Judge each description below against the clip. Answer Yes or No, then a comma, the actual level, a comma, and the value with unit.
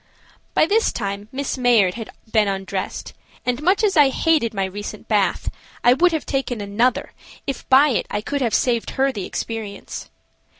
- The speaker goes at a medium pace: Yes, average, 175 wpm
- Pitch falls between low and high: No, high, 245 Hz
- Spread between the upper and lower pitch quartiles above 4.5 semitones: Yes, average, 5.3 semitones